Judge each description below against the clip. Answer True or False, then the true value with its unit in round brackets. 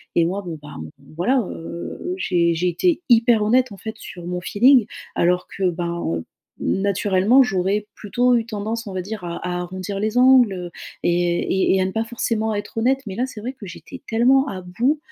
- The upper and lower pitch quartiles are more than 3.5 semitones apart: True (4.9 semitones)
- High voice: True (200 Hz)